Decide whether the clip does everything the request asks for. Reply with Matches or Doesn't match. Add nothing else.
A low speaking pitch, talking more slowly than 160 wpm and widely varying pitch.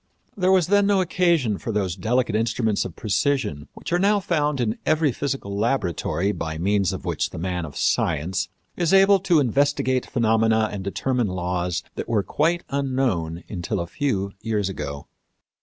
Doesn't match